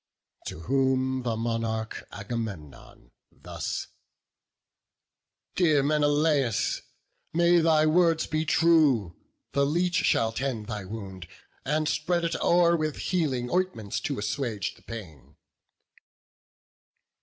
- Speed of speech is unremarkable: No, slow, 105 wpm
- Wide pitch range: Yes, wide, 6.2 semitones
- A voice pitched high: No, low, 135 Hz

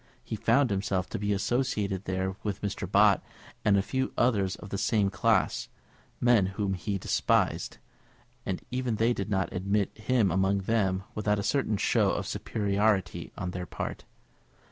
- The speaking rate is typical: Yes, average, 165 wpm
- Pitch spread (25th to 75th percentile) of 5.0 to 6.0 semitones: No, narrow, 2.4 semitones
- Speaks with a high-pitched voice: No, low, 100 Hz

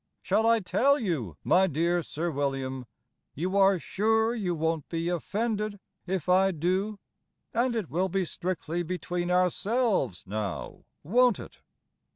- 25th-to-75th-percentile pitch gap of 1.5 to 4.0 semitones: No, average, 4.4 semitones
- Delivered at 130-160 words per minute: Yes, average, 140 wpm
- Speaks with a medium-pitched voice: Yes, medium, 180 Hz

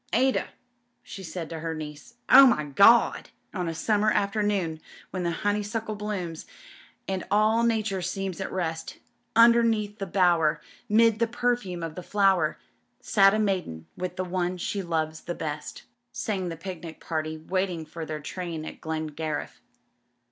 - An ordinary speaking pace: Yes, average, 160 wpm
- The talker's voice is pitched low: No, medium, 185 Hz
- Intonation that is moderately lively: Yes, average, 4.4 semitones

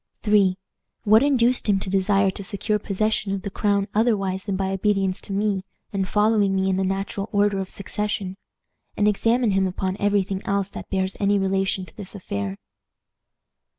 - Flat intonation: Yes, narrow, 1.5 semitones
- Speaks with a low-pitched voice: No, high, 195 Hz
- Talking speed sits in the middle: Yes, average, 180 wpm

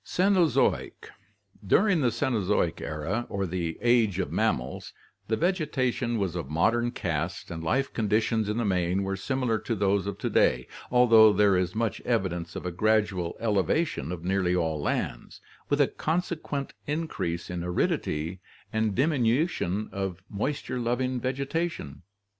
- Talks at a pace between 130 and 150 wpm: Yes, average, 145 wpm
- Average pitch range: No, wide, 6.0 semitones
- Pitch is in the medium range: No, low, 105 Hz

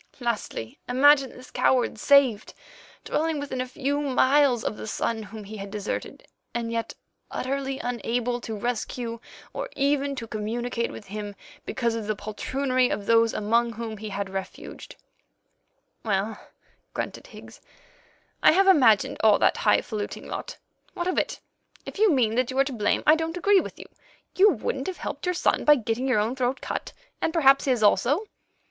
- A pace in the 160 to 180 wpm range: Yes, average, 175 wpm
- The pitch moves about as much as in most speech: Yes, average, 4.2 semitones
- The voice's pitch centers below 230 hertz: No, high, 245 Hz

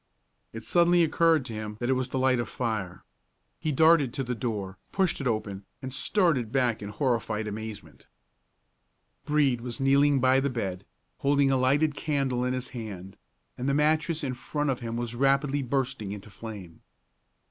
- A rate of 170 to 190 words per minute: Yes, average, 175 wpm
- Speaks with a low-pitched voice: Yes, low, 130 Hz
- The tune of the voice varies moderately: Yes, average, 4.1 semitones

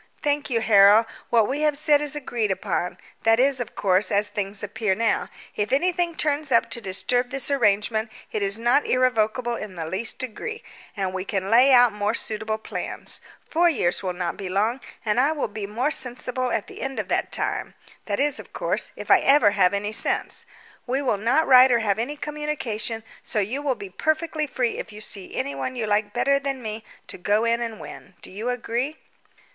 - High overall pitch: Yes, high, 230 Hz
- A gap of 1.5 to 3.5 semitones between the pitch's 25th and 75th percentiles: No, average, 4.6 semitones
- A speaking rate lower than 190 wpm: No, fast, 205 wpm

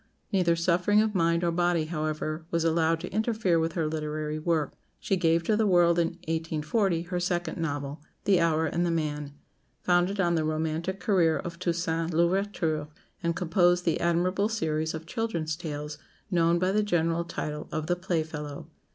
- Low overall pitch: No, medium, 170 Hz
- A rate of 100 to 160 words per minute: No, average, 170 wpm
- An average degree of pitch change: No, narrow, 2.0 semitones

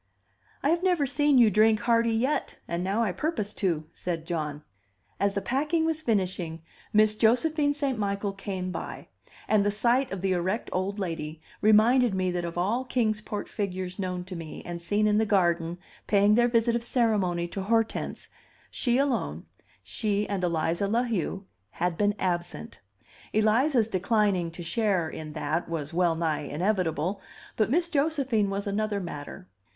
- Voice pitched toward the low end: No, high, 205 Hz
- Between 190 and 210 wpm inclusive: No, average, 165 wpm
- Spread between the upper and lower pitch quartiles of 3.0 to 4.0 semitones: No, average, 4.6 semitones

